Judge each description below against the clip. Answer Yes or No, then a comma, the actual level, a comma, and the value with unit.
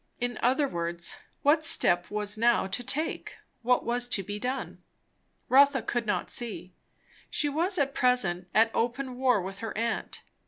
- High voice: Yes, high, 240 Hz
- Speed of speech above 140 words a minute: Yes, average, 160 wpm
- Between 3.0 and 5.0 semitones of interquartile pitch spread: Yes, average, 4.2 semitones